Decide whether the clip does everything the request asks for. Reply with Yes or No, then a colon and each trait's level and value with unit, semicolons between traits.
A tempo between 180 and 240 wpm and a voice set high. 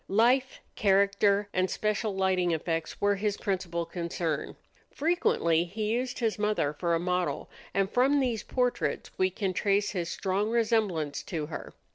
No: average, 150 wpm; high, 195 Hz